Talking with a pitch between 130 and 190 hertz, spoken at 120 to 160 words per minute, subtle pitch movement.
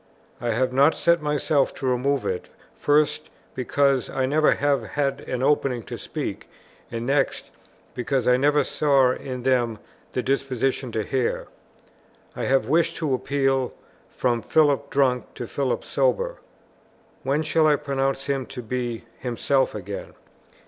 Yes: low, 135 Hz; average, 145 wpm; narrow, 2.2 semitones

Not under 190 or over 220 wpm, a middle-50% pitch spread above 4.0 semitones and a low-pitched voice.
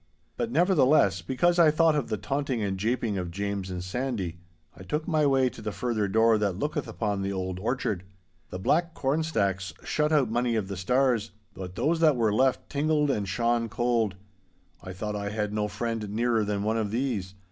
Yes: average, 200 wpm; average, 5.2 semitones; low, 110 Hz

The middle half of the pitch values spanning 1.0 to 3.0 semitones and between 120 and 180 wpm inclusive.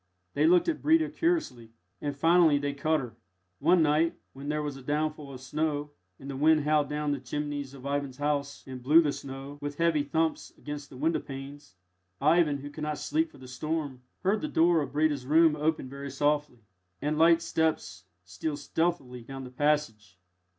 No: narrow, 2.5 semitones; average, 190 wpm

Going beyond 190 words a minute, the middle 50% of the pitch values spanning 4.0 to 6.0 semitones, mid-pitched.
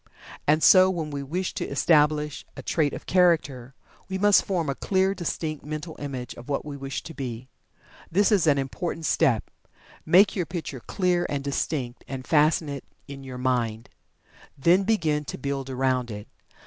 No: average, 175 wpm; average, 4.3 semitones; medium, 150 Hz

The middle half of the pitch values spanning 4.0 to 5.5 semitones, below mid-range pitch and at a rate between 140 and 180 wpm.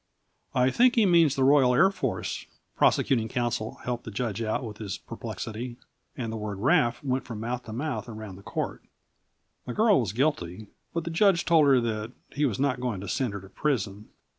No: average, 4.6 semitones; low, 120 Hz; average, 200 wpm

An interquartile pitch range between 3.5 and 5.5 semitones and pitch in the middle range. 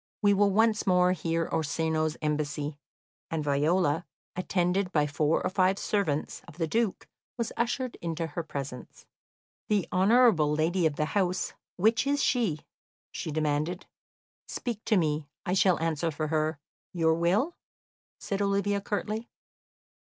Yes: average, 4.5 semitones; medium, 175 Hz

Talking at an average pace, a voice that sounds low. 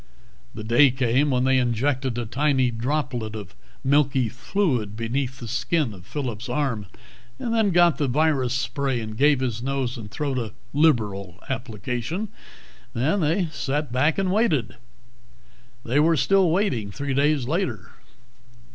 Yes: average, 145 wpm; low, 130 Hz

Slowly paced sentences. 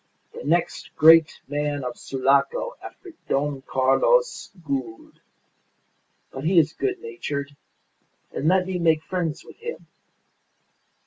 Yes: slow, 120 wpm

